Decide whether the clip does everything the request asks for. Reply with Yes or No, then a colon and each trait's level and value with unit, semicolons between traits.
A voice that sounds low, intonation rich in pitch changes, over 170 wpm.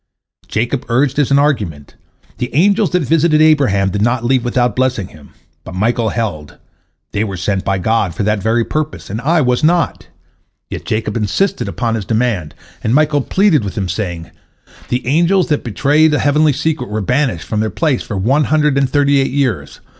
Yes: low, 125 Hz; wide, 6.0 semitones; average, 190 wpm